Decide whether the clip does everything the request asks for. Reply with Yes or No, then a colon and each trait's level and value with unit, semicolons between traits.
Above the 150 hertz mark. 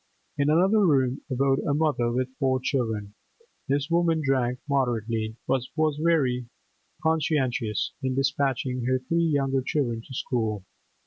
No: low, 135 Hz